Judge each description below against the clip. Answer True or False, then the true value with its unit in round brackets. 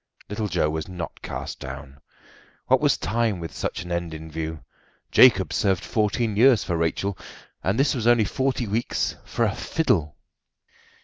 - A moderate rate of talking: True (165 wpm)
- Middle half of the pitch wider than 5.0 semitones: True (5.6 semitones)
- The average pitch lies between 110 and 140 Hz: False (95 Hz)